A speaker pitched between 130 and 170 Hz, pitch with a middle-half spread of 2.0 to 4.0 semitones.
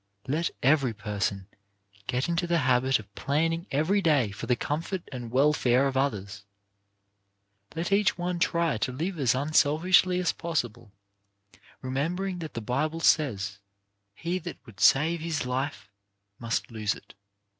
No: medium, 140 Hz; wide, 5.6 semitones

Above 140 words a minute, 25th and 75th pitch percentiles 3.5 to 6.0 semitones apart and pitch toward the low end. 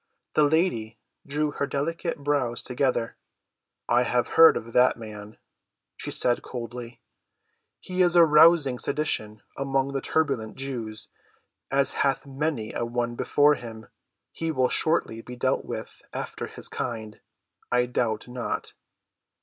No: slow, 135 wpm; average, 3.9 semitones; low, 125 Hz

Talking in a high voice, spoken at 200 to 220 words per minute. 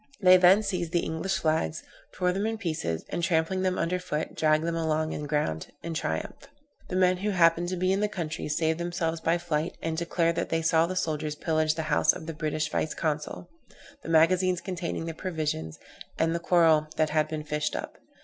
No: medium, 165 Hz; fast, 205 wpm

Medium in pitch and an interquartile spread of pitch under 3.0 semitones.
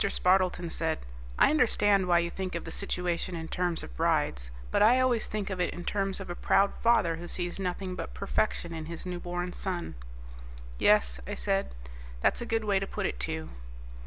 Yes: medium, 180 Hz; narrow, 2.6 semitones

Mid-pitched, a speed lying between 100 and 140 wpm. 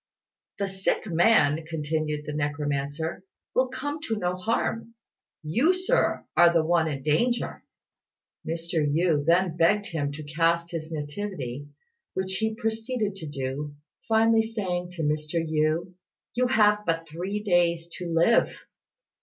Yes: medium, 170 Hz; slow, 135 wpm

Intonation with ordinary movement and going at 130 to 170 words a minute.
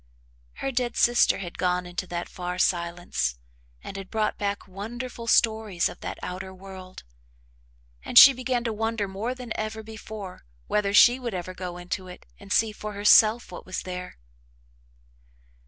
Yes: average, 3.6 semitones; average, 160 wpm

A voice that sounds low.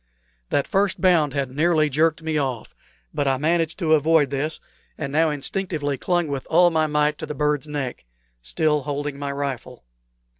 No: medium, 150 Hz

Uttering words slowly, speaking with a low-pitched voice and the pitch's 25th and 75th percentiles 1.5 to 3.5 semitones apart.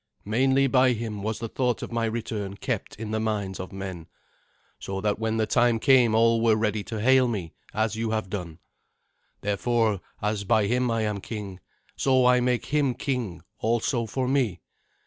No: average, 185 wpm; low, 110 Hz; average, 2.9 semitones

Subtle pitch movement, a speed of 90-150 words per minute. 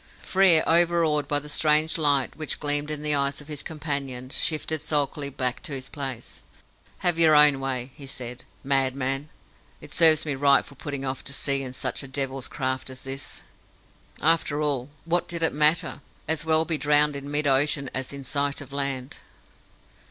No: narrow, 2.2 semitones; average, 180 wpm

